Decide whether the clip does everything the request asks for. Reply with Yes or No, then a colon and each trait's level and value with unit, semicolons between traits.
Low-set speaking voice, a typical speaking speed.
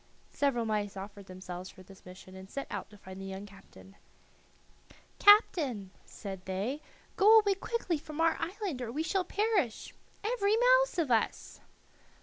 No: high, 245 Hz; average, 155 wpm